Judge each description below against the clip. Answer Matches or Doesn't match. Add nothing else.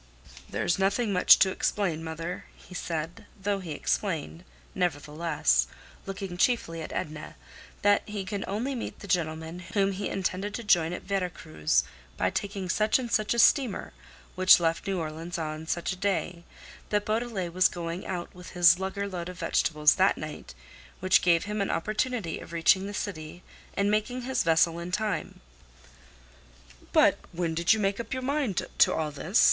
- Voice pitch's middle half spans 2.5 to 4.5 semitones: Matches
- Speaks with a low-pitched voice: Doesn't match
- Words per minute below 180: Matches